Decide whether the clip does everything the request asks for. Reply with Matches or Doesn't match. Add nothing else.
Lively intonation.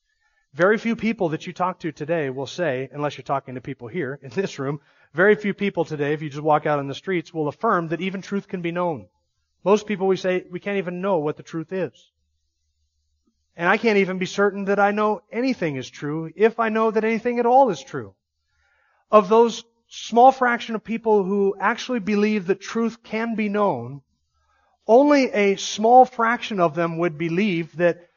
Matches